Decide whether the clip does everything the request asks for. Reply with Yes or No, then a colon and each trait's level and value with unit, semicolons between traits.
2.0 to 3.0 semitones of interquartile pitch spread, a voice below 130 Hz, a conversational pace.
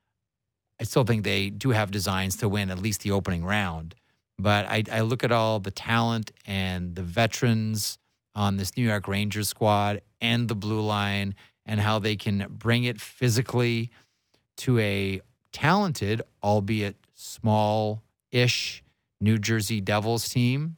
Yes: narrow, 2.5 semitones; low, 110 Hz; average, 150 wpm